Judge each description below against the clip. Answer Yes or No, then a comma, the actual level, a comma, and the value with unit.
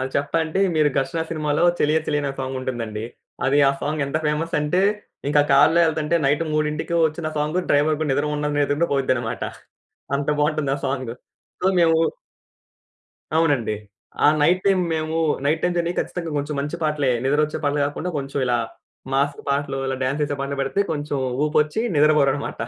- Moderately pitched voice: Yes, medium, 150 Hz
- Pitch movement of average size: No, narrow, 2.1 semitones